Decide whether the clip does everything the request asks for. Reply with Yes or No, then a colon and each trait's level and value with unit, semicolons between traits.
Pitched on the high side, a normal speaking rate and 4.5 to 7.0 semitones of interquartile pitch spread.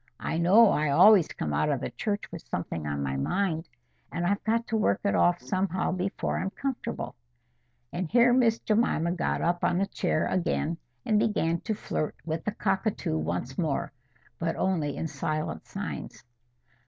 No: medium, 175 Hz; average, 175 wpm; average, 5.1 semitones